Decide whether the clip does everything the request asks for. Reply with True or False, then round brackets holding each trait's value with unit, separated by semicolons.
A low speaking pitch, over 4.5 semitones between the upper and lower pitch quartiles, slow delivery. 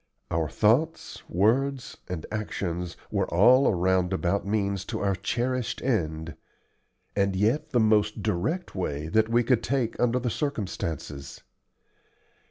True (105 Hz; 5.3 semitones; 130 wpm)